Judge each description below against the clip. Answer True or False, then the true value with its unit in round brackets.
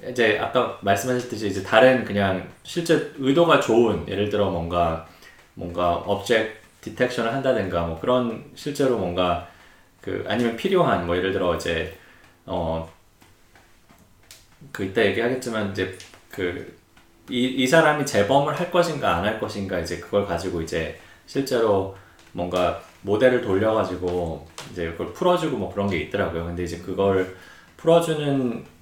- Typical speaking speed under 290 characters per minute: False (295 characters per minute)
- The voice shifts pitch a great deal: True (6.2 semitones)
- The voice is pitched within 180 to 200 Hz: False (100 Hz)